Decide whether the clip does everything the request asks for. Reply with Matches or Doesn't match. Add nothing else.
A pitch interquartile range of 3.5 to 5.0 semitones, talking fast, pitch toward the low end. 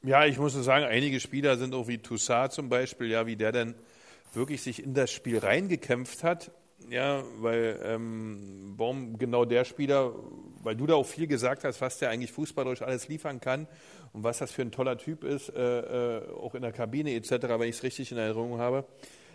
Doesn't match